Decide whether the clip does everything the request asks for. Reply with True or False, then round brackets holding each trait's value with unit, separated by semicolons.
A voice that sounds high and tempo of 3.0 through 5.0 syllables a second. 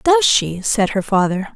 True (210 Hz; 4.1 syllables/s)